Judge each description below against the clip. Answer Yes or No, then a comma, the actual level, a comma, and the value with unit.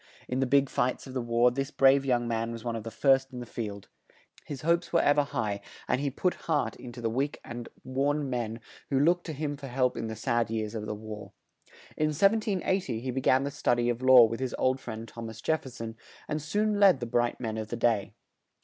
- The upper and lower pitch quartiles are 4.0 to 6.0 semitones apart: No, average, 3.6 semitones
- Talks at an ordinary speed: No, fast, 250 wpm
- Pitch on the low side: Yes, low, 125 Hz